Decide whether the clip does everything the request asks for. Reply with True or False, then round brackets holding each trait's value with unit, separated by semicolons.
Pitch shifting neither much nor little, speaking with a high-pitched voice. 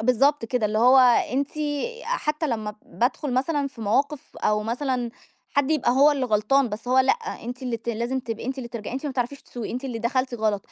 True (3.4 semitones; 255 Hz)